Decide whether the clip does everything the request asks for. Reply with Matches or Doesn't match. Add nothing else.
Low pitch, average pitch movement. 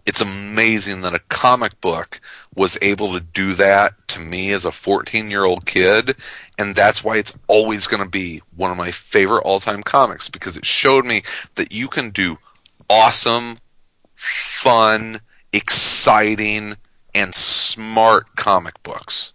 Doesn't match